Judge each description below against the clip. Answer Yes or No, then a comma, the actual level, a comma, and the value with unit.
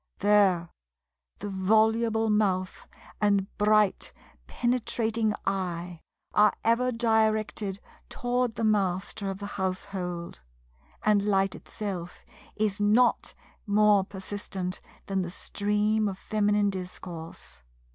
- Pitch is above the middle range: Yes, high, 205 Hz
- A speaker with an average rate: No, slow, 100 wpm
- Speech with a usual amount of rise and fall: No, narrow, 2.3 semitones